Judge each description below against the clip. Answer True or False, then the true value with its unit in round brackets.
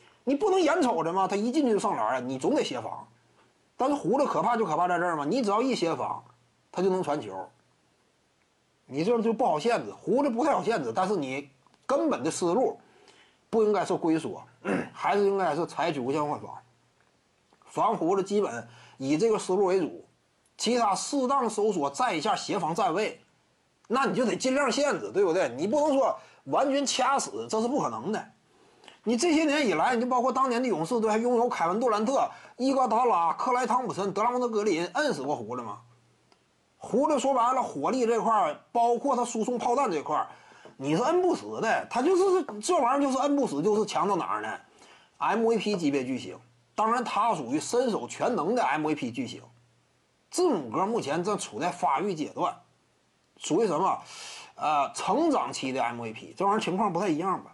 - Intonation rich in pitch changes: True (6.0 semitones)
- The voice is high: True (235 Hz)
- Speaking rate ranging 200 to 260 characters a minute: False (290 characters per minute)